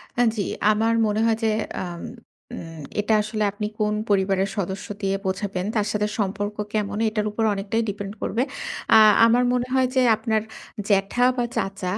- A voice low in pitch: No, high, 210 Hz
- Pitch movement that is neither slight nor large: No, narrow, 2.0 semitones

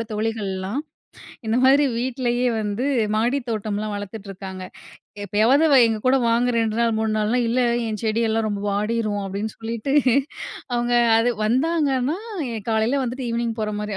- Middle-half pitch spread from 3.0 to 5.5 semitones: No, narrow, 2.6 semitones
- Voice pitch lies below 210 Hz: No, high, 225 Hz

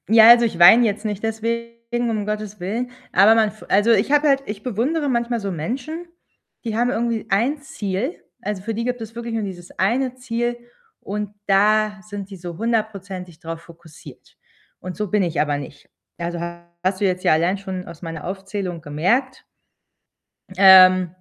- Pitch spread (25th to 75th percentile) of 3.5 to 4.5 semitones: Yes, average, 4.1 semitones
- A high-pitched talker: Yes, high, 210 Hz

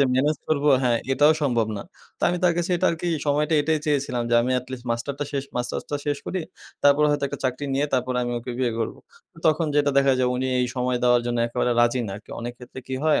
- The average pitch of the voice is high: No, low, 130 Hz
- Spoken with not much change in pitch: No, average, 3.1 semitones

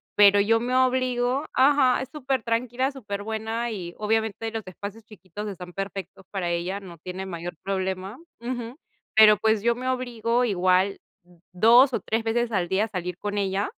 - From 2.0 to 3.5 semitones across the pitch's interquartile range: No, average, 4.0 semitones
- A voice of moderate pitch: No, high, 220 Hz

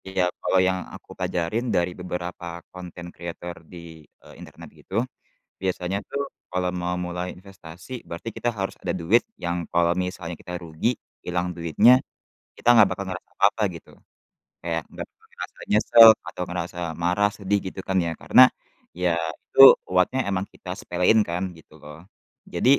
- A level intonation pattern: Yes, narrow, 2.2 semitones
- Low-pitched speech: Yes, very low, 90 Hz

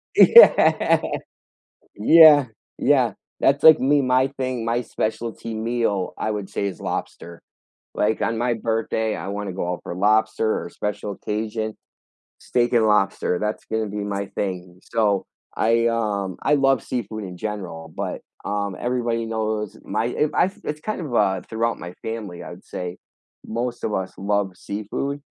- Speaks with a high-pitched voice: No, low, 110 Hz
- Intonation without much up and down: No, average, 3.0 semitones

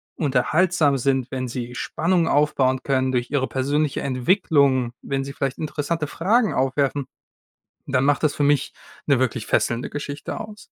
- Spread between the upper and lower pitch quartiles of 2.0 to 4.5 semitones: Yes, narrow, 2.6 semitones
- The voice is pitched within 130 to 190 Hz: Yes, medium, 140 Hz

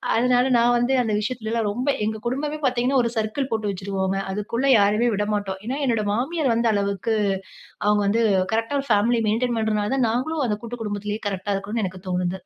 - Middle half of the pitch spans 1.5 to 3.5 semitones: Yes, average, 2.9 semitones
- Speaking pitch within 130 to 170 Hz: No, high, 220 Hz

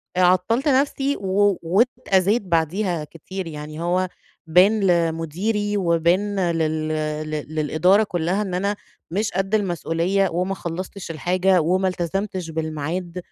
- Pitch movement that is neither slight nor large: Yes, average, 3.1 semitones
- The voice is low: No, medium, 180 Hz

